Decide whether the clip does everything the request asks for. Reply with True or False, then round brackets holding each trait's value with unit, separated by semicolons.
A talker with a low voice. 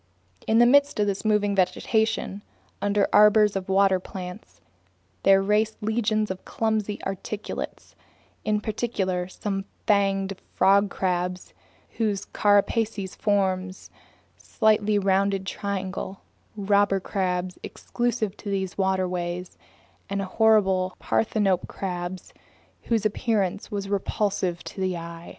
False (200 Hz)